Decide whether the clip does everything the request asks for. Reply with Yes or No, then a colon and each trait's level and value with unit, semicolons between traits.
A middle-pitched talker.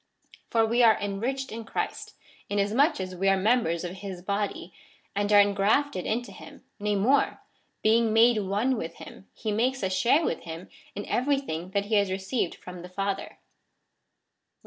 No: high, 205 Hz